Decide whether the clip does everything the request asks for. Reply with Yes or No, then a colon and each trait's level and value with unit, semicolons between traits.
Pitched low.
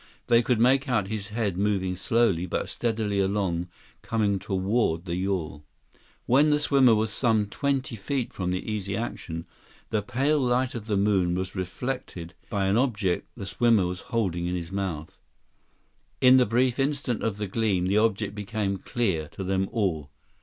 Yes: low, 105 Hz